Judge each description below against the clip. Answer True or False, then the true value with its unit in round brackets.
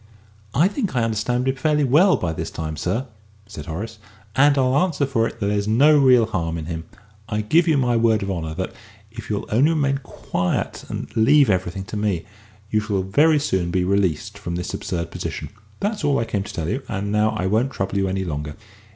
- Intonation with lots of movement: True (6.4 semitones)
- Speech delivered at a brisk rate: True (215 wpm)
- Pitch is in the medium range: False (105 Hz)